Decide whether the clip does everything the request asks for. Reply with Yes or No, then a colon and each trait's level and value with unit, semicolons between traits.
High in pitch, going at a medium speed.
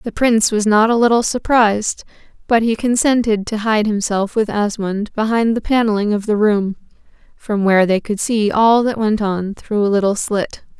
Yes: high, 215 Hz; average, 190 wpm